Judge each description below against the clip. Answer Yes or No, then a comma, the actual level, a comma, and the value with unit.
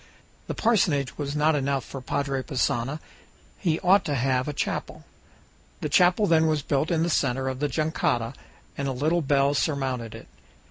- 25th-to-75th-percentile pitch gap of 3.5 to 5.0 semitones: No, average, 3.0 semitones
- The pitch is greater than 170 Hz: No, medium, 145 Hz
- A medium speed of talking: Yes, average, 175 wpm